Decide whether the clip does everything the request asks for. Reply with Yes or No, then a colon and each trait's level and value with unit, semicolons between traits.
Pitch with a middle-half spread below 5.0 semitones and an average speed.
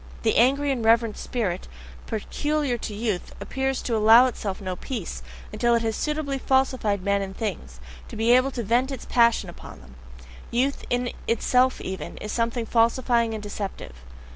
Yes: average, 3.7 semitones; average, 165 wpm